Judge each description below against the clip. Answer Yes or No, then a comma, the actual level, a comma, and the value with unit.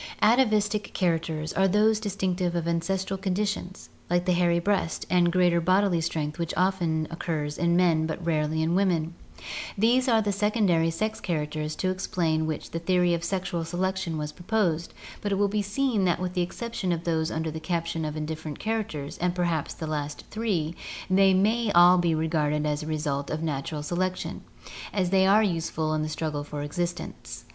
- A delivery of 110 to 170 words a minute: No, average, 185 wpm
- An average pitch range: Yes, average, 3.3 semitones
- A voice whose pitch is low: No, medium, 175 Hz